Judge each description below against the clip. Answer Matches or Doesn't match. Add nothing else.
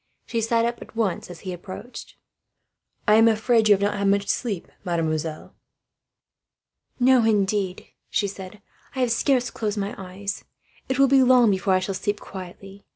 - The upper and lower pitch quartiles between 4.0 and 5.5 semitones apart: Doesn't match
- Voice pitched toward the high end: Matches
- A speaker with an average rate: Matches